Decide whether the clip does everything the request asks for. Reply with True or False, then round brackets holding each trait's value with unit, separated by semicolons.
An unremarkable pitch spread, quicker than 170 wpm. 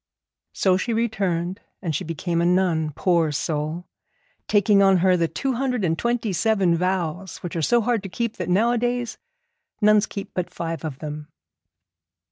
False (4.8 semitones; 165 wpm)